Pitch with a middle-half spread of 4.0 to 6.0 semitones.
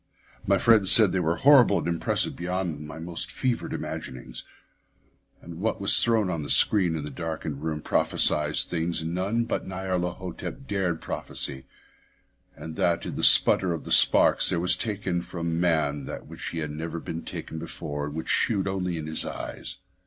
No: average, 3.1 semitones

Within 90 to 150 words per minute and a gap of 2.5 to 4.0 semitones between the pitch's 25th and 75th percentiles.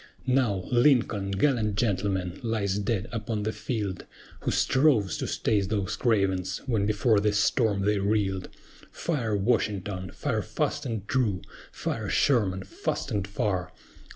Yes: slow, 135 wpm; average, 2.9 semitones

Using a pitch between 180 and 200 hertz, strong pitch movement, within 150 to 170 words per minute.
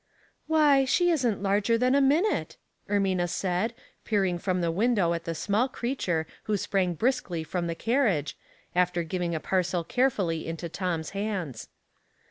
Yes: high, 190 Hz; wide, 5.8 semitones; average, 160 wpm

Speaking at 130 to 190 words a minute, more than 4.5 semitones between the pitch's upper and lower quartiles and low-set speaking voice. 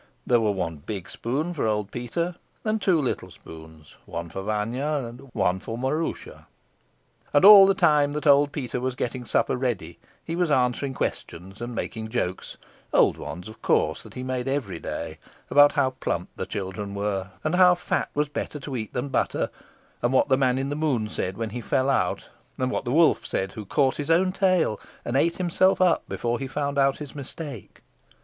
No: average, 200 wpm; wide, 5.4 semitones; low, 130 Hz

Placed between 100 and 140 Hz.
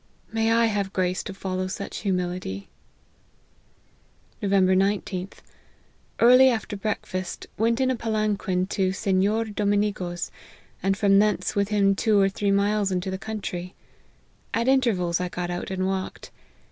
No: high, 195 Hz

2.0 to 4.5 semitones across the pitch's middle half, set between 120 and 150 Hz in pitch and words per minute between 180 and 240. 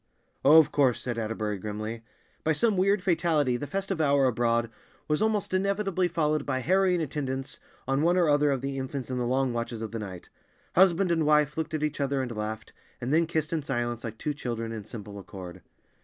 No: wide, 5.5 semitones; medium, 140 Hz; fast, 205 wpm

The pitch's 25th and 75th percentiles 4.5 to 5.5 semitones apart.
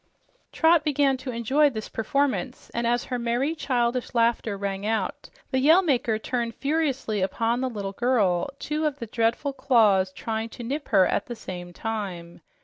No: average, 4.1 semitones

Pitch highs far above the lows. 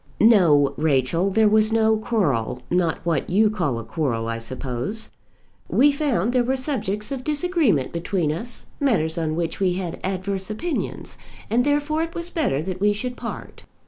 Yes: wide, 7.5 semitones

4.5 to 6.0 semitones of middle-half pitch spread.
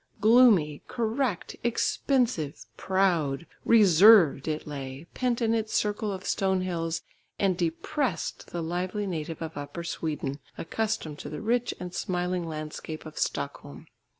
Yes: wide, 5.6 semitones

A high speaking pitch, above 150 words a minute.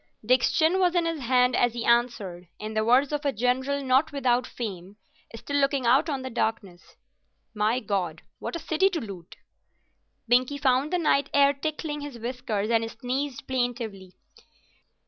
Yes: very high, 250 Hz; average, 165 wpm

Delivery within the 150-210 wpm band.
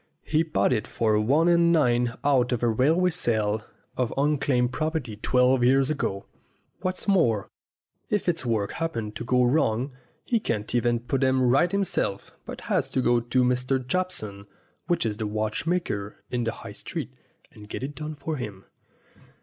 Yes: average, 175 wpm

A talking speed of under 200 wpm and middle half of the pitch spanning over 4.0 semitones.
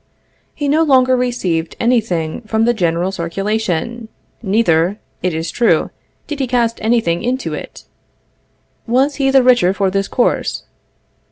Yes: average, 150 wpm; wide, 5.5 semitones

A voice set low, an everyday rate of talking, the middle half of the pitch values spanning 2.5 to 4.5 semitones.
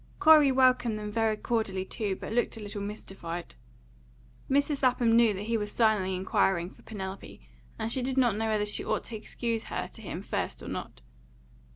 No: high, 220 Hz; average, 190 wpm; average, 3.1 semitones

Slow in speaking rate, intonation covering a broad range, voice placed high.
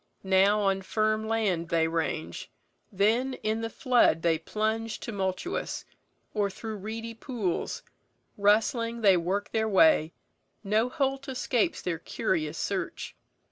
No: slow, 125 wpm; average, 3.3 semitones; high, 210 Hz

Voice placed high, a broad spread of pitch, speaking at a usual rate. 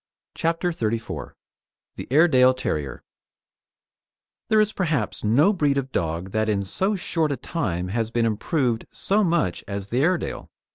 No: low, 130 Hz; wide, 7.8 semitones; average, 145 wpm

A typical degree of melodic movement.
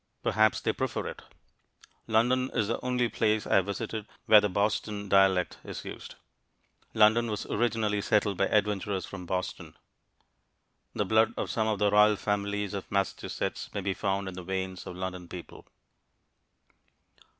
No: narrow, 2.1 semitones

